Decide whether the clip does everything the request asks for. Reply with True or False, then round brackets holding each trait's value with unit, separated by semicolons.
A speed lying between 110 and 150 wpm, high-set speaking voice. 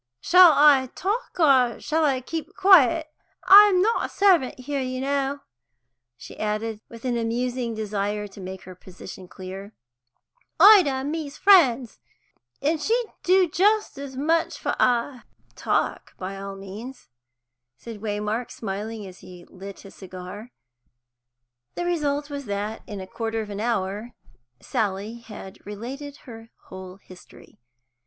True (140 wpm; 240 Hz)